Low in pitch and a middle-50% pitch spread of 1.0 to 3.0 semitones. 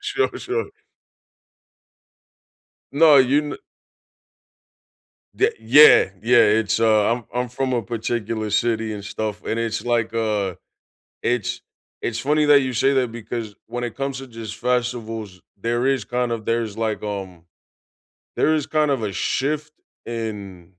No: low, 115 Hz; average, 3.5 semitones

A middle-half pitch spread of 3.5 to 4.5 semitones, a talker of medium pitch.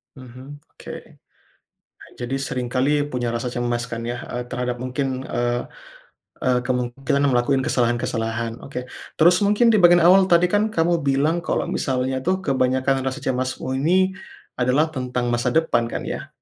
No: average, 4.2 semitones; low, 130 Hz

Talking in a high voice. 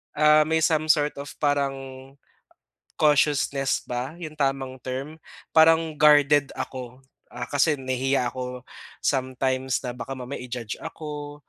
No: medium, 140 Hz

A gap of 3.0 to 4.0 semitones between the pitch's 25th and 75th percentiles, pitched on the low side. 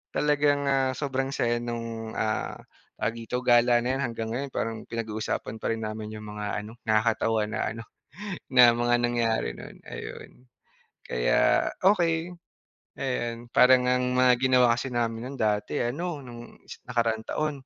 No: narrow, 2.5 semitones; low, 120 Hz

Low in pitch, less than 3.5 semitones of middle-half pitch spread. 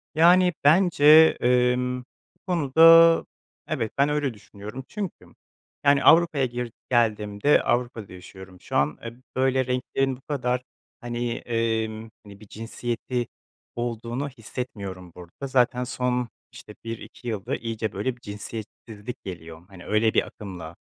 No: low, 120 Hz; average, 3.8 semitones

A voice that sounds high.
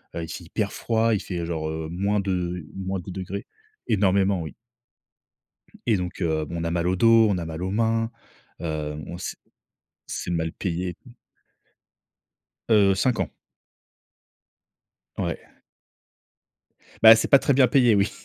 No: very low, 95 Hz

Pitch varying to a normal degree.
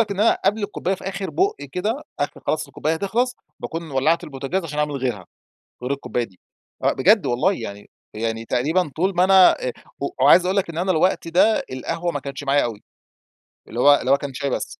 No: wide, 6.0 semitones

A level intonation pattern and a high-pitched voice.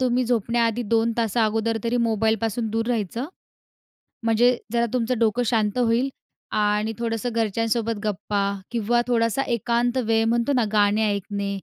Yes: narrow, 1.8 semitones; high, 230 Hz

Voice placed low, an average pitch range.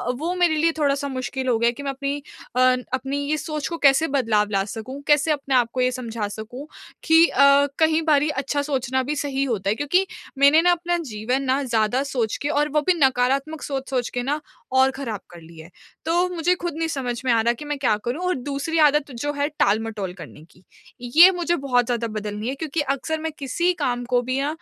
No: very high, 275 Hz; average, 3.6 semitones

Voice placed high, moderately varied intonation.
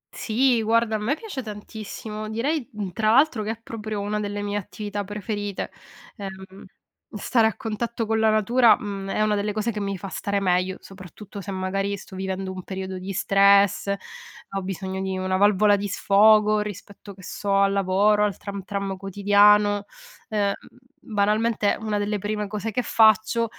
No: high, 205 Hz; narrow, 1.6 semitones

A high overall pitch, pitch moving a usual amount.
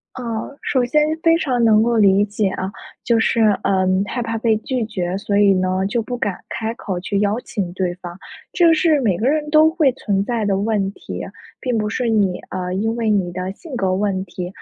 Yes: high, 215 Hz; average, 4.1 semitones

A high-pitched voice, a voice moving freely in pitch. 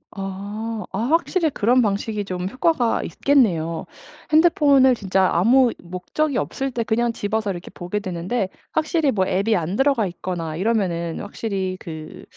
Yes: high, 210 Hz; wide, 5.8 semitones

